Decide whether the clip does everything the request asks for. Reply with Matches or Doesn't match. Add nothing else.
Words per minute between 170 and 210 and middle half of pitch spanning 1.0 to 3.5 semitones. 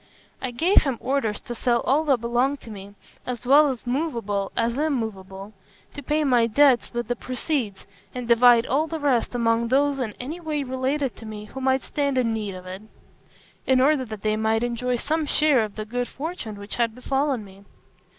Doesn't match